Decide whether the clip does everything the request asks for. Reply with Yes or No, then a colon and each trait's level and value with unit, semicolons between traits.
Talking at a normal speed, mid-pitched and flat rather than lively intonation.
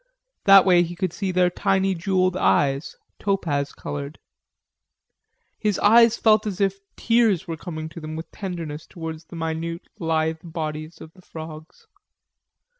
No: average, 145 wpm; medium, 170 Hz; average, 3.5 semitones